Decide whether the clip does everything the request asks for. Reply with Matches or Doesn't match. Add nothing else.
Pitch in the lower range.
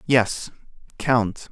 Matches